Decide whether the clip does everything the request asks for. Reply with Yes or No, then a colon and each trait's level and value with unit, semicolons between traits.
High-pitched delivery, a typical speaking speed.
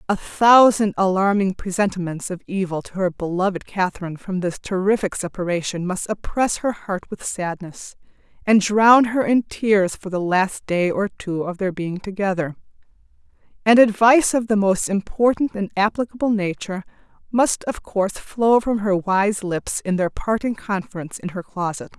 Yes: high, 195 Hz; average, 160 wpm